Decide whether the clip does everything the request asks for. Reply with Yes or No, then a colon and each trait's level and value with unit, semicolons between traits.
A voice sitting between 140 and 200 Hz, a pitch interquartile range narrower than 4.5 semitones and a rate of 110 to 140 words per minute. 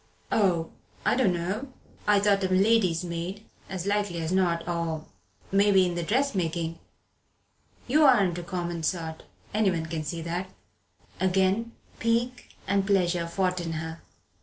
Yes: medium, 185 Hz; average, 3.1 semitones; slow, 135 wpm